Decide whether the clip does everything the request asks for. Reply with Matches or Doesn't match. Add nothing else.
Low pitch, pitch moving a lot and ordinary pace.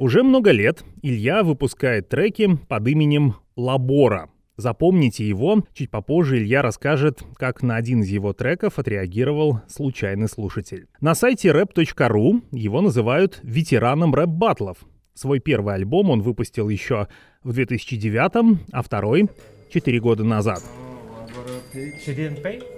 Matches